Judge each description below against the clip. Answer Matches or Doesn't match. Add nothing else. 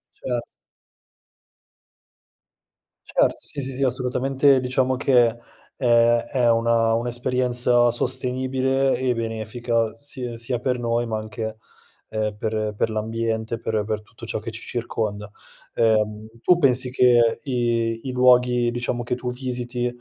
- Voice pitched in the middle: Doesn't match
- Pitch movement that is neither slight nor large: Doesn't match